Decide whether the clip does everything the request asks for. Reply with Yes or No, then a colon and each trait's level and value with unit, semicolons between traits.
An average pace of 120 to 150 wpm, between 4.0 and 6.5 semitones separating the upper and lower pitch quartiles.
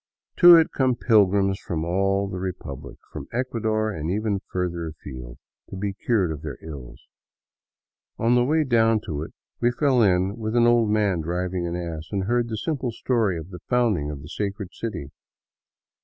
No: average, 180 wpm; average, 5.2 semitones